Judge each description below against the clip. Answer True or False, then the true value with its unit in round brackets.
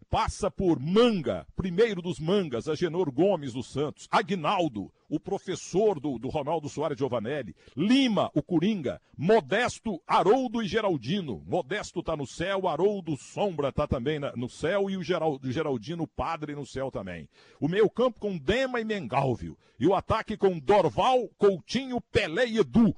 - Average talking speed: True (160 wpm)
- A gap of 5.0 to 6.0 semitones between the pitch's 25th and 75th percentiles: True (5.5 semitones)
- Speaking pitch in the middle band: True (180 Hz)